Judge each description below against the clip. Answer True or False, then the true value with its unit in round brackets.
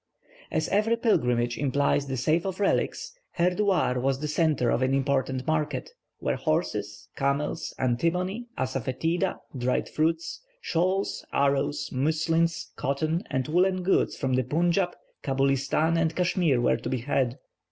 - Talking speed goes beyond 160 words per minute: False (135 wpm)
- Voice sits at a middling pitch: True (150 Hz)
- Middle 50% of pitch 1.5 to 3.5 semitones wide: False (4.7 semitones)